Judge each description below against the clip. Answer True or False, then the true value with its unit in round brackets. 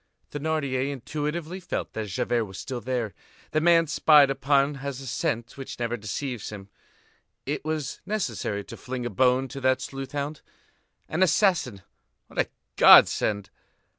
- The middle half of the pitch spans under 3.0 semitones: False (3.9 semitones)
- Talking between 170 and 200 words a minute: False (150 wpm)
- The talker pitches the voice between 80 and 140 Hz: True (135 Hz)